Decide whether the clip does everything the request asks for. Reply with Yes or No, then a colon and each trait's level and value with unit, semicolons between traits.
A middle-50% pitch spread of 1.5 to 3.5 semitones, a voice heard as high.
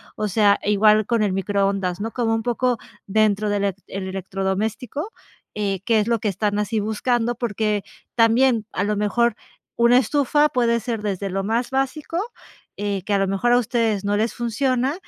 Yes: average, 2.9 semitones; high, 215 Hz